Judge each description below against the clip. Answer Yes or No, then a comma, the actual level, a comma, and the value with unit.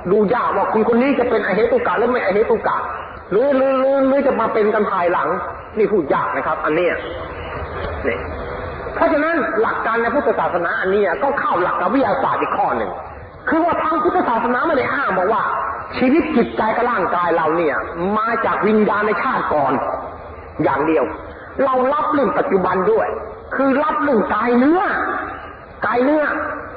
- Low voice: No, very high, 265 Hz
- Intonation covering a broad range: Yes, wide, 6.1 semitones